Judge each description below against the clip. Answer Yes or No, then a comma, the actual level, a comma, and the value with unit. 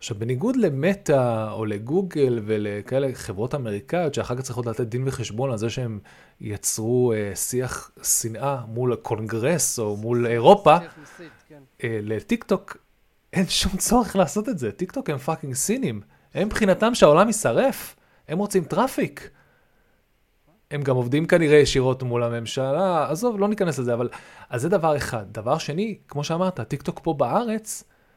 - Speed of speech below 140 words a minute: No, average, 145 wpm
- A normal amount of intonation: No, wide, 8.1 semitones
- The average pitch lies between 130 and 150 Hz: Yes, medium, 140 Hz